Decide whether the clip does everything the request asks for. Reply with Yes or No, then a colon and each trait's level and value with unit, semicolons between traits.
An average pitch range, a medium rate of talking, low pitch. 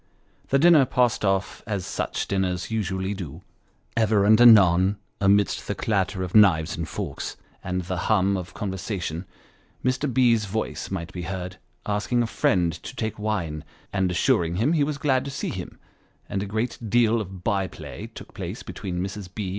Yes: average, 3.4 semitones; average, 180 wpm; low, 100 Hz